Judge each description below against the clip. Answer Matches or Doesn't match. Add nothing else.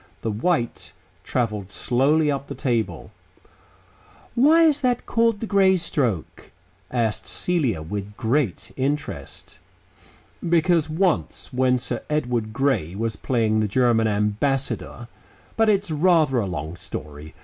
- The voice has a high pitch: Doesn't match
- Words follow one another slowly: Matches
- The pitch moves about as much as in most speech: Doesn't match